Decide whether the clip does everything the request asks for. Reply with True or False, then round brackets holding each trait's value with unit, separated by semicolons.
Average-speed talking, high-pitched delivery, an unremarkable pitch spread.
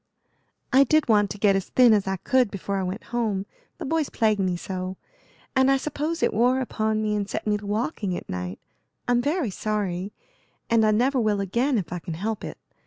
False (215 wpm; 215 Hz; 4.3 semitones)